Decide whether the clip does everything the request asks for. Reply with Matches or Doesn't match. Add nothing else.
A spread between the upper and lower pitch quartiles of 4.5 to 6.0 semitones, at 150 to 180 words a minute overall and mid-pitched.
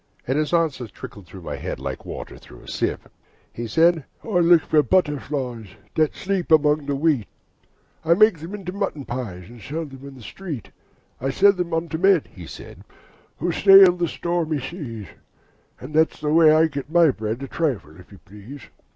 Doesn't match